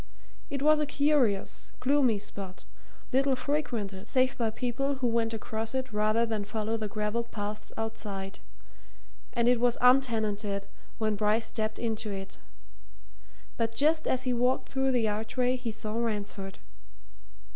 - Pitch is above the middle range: Yes, high, 225 Hz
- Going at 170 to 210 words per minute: No, average, 145 wpm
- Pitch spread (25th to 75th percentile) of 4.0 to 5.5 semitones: No, average, 3.3 semitones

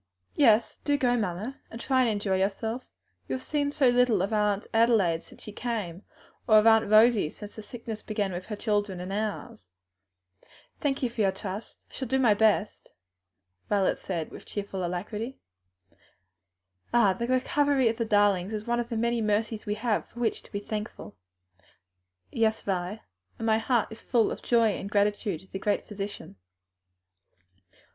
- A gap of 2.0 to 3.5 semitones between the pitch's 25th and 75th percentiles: Yes, average, 2.9 semitones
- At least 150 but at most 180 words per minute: Yes, average, 175 wpm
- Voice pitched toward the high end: Yes, high, 215 Hz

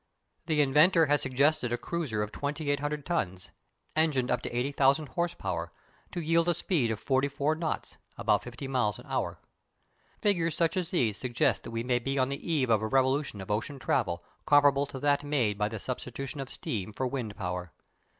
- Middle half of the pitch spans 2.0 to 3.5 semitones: No, average, 4.2 semitones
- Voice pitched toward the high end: No, low, 135 Hz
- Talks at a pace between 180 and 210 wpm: Yes, average, 190 wpm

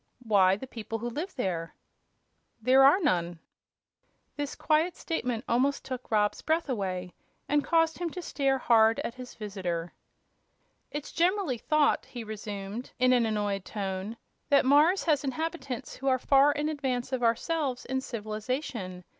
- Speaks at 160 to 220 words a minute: No, average, 150 wpm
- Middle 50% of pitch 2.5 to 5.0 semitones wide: No, wide, 5.5 semitones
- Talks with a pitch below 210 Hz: No, very high, 250 Hz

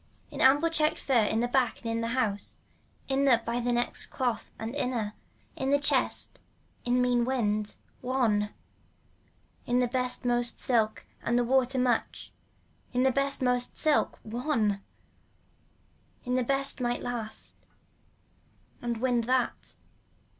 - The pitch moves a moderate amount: No, narrow, 2.0 semitones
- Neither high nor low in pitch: No, high, 245 Hz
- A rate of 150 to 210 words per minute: No, average, 140 wpm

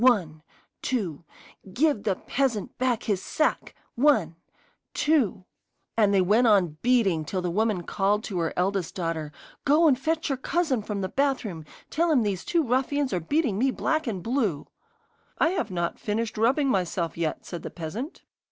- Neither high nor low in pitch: No, high, 215 Hz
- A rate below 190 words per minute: Yes, average, 170 wpm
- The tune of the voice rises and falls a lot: Yes, wide, 6.9 semitones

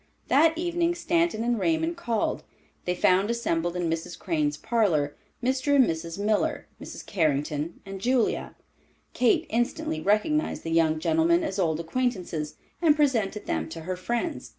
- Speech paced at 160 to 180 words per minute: No, average, 150 wpm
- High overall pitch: Yes, high, 210 Hz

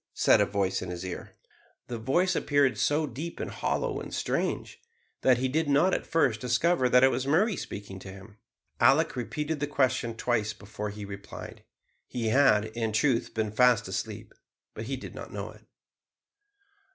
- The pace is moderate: Yes, average, 175 wpm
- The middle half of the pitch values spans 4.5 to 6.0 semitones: Yes, average, 5.1 semitones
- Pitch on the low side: Yes, low, 125 Hz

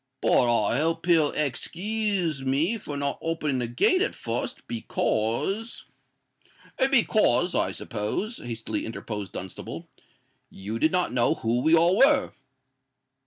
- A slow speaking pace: Yes, slow, 130 wpm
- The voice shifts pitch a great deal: Yes, wide, 7.9 semitones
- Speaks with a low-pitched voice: No, medium, 150 Hz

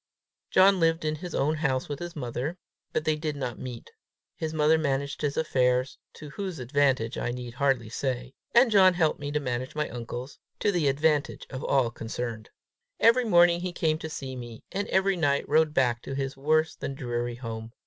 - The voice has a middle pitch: Yes, medium, 145 Hz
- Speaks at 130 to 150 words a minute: No, average, 195 wpm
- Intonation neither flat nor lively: Yes, average, 4.2 semitones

